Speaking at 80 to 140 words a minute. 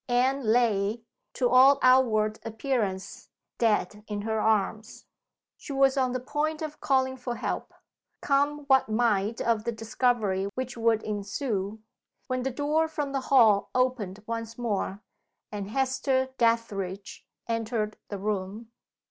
Yes: slow, 135 wpm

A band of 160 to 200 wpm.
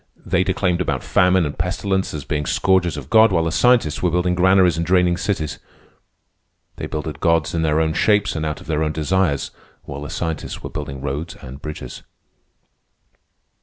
Yes: average, 180 wpm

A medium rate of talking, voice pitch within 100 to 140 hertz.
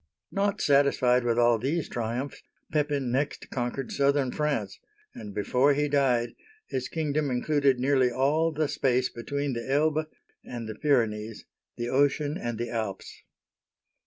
Yes: average, 145 wpm; low, 135 Hz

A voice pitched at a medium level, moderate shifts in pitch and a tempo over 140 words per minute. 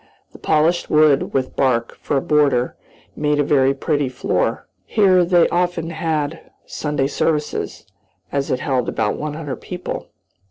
Yes: medium, 150 Hz; average, 3.3 semitones; average, 150 wpm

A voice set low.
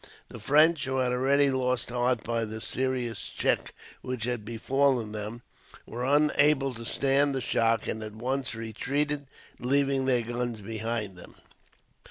Yes: low, 125 Hz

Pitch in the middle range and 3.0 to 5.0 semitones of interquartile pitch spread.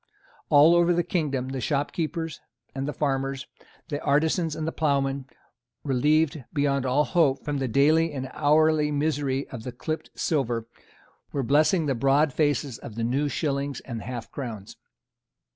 No: medium, 145 Hz; narrow, 2.6 semitones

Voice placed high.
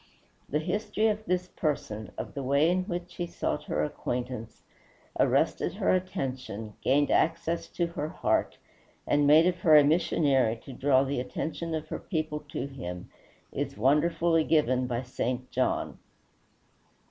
No: medium, 150 Hz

